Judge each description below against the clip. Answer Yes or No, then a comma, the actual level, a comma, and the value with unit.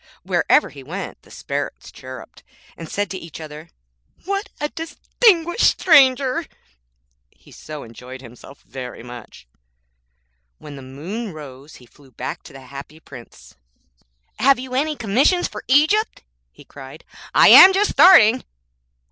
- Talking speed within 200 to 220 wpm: No, average, 140 wpm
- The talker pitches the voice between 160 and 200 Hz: Yes, high, 190 Hz